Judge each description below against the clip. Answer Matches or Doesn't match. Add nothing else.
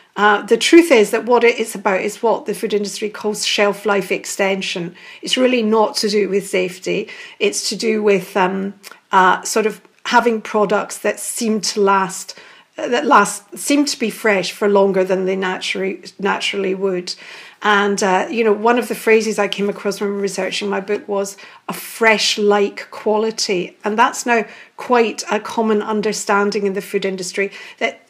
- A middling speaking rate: Matches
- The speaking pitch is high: Matches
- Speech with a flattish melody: Matches